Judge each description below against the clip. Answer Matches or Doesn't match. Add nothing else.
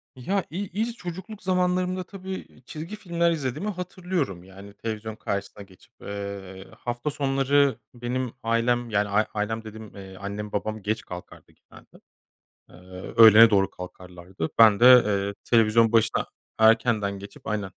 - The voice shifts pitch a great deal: Matches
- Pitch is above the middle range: Doesn't match